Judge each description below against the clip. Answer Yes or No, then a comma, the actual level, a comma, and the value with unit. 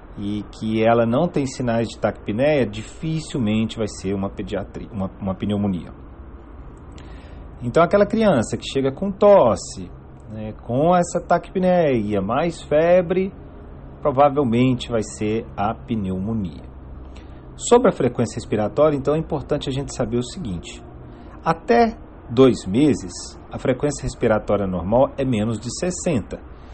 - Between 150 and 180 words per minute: No, average, 125 wpm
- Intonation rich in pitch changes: Yes, wide, 7.6 semitones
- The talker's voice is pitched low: Yes, low, 115 Hz